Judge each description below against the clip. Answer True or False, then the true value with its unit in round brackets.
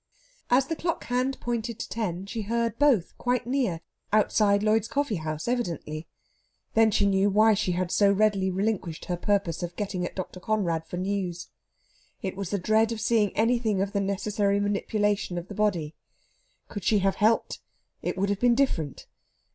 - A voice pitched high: True (205 Hz)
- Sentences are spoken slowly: False (175 wpm)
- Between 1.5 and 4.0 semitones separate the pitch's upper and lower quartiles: True (3.3 semitones)